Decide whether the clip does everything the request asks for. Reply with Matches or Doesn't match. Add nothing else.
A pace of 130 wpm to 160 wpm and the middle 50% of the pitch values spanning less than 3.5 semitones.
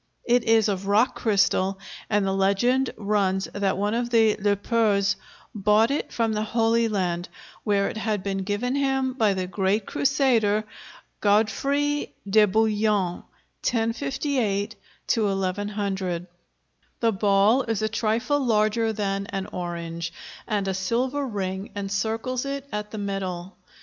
Matches